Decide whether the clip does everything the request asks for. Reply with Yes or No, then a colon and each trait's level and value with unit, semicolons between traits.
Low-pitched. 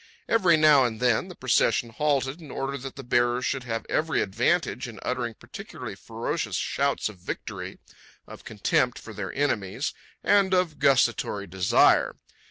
Yes: low, 125 Hz